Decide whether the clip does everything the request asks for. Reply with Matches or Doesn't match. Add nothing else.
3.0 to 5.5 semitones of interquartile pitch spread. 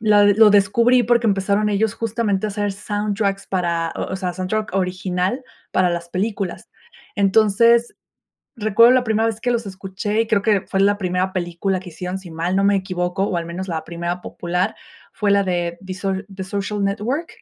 Doesn't match